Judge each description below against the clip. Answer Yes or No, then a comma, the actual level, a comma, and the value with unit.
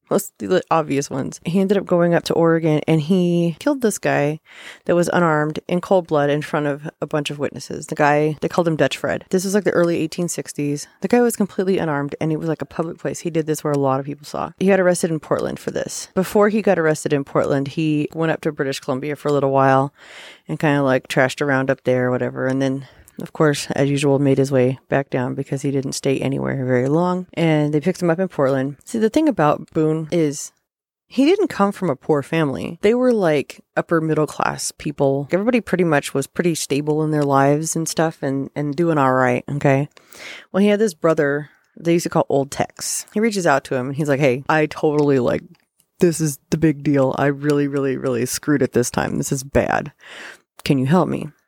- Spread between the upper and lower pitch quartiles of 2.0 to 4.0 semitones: Yes, average, 3.7 semitones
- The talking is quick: Yes, fast, 235 wpm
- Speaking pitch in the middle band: Yes, medium, 150 Hz